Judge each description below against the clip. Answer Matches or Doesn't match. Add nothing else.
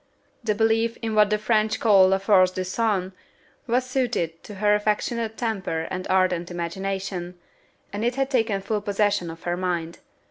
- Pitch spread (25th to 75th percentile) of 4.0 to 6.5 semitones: Doesn't match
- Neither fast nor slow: Matches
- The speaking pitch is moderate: Doesn't match